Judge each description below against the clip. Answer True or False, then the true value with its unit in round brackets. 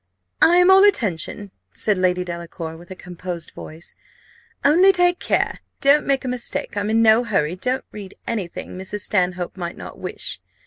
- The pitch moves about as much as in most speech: False (6.7 semitones)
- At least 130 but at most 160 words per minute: False (175 wpm)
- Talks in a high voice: True (205 Hz)